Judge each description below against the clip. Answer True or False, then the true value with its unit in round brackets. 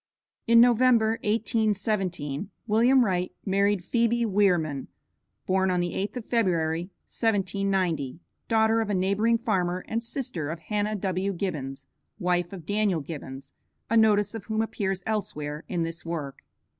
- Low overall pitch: False (195 Hz)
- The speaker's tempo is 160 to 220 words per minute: False (140 wpm)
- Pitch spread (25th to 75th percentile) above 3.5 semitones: True (4.2 semitones)